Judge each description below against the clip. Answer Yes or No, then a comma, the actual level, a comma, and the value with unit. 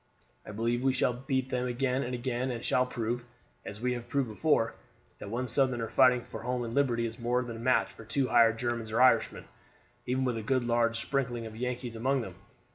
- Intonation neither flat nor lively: No, narrow, 1.7 semitones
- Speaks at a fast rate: Yes, fast, 215 wpm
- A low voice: Yes, low, 120 Hz